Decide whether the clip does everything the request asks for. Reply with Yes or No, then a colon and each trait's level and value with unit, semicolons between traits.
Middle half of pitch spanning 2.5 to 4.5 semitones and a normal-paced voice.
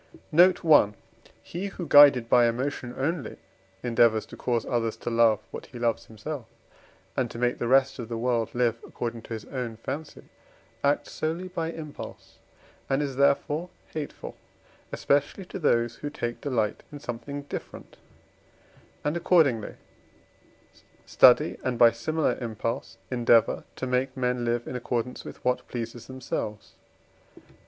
Yes: average, 3.6 semitones; average, 145 wpm